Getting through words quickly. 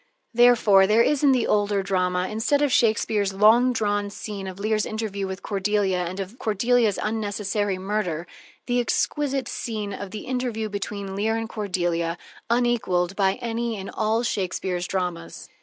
No: average, 155 wpm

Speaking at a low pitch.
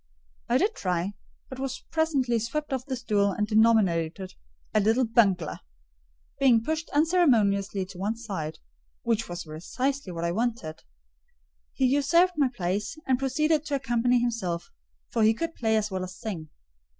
No: high, 225 Hz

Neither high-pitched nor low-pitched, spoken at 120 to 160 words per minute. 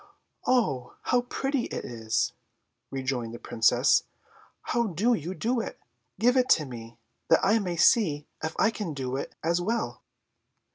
Yes: medium, 170 Hz; average, 155 wpm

